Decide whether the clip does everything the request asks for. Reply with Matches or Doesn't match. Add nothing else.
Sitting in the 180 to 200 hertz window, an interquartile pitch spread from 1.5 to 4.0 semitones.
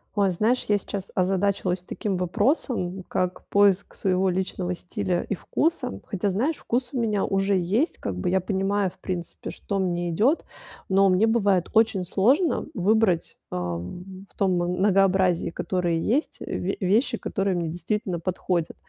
Matches